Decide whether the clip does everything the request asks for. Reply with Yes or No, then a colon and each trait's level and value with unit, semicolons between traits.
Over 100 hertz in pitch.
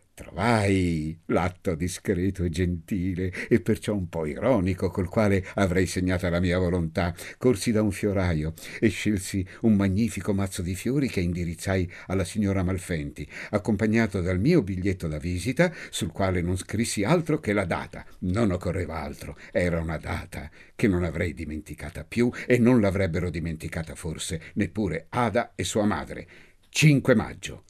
No: very low, 95 Hz